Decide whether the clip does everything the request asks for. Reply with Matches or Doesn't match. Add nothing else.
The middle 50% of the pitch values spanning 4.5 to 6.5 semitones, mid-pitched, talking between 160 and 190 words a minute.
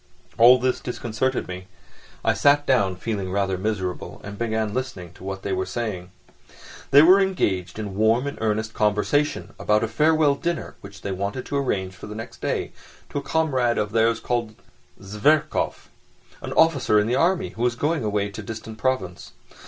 Doesn't match